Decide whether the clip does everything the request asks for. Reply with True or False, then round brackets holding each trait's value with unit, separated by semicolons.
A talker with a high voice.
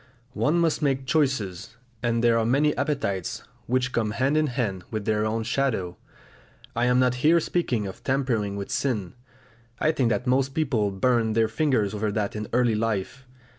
False (120 Hz)